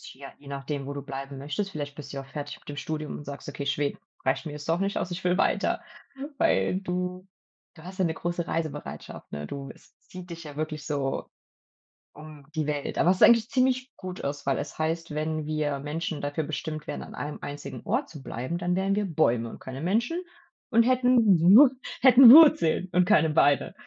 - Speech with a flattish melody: No, average, 4.3 semitones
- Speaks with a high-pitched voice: No, medium, 155 Hz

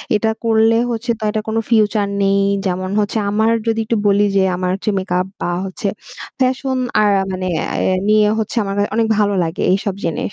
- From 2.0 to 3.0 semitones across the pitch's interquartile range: Yes, narrow, 2.6 semitones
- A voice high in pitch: Yes, high, 210 Hz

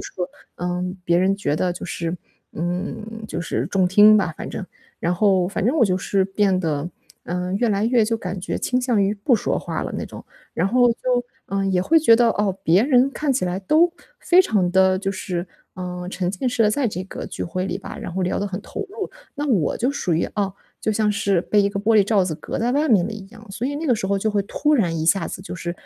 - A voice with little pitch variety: No, average, 3.8 semitones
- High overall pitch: Yes, high, 200 Hz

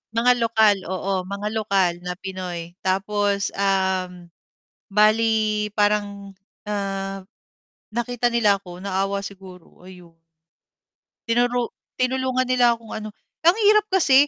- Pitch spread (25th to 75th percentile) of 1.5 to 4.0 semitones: Yes, average, 3.5 semitones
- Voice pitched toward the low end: No, high, 205 Hz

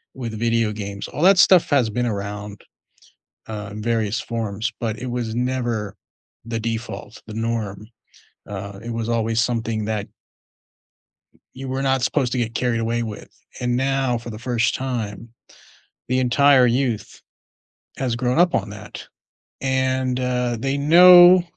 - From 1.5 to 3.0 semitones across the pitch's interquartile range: Yes, average, 2.7 semitones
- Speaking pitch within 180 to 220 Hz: No, low, 120 Hz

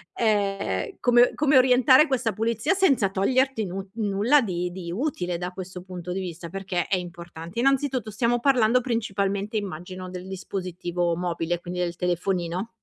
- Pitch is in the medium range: No, high, 195 Hz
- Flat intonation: No, average, 4.8 semitones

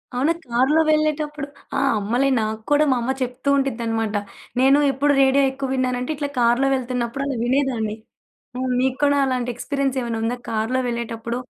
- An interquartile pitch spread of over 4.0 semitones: No, average, 2.8 semitones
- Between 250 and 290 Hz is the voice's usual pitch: Yes, very high, 255 Hz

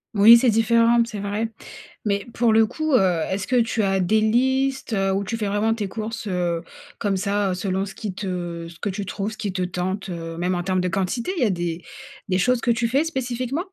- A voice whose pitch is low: No, high, 205 Hz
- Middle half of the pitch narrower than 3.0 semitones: No, average, 3.9 semitones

